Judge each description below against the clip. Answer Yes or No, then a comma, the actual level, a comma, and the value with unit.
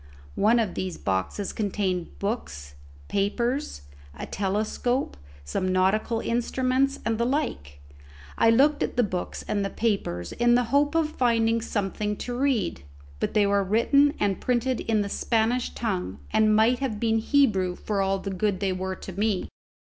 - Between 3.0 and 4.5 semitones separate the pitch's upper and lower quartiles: Yes, average, 4.0 semitones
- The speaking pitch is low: No, high, 215 Hz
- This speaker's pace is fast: No, average, 160 wpm